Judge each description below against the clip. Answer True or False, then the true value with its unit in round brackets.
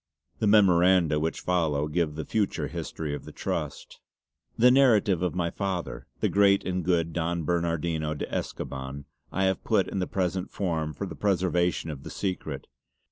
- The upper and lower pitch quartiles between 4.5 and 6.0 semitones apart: False (3.3 semitones)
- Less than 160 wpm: False (175 wpm)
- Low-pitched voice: True (85 Hz)